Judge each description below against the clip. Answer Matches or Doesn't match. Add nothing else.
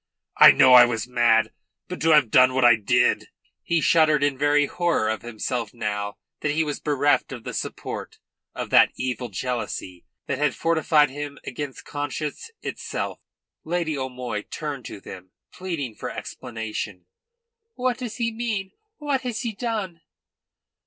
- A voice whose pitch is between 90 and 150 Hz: Matches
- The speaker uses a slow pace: Doesn't match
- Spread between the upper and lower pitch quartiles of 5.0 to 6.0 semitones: Matches